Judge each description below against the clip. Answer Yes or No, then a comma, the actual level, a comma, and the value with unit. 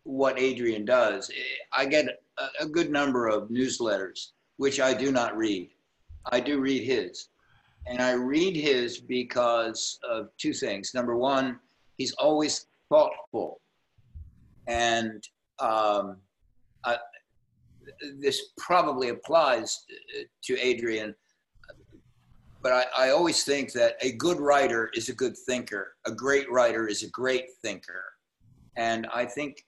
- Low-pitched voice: Yes, low, 125 Hz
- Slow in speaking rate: Yes, slow, 130 wpm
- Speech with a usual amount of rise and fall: Yes, average, 3.7 semitones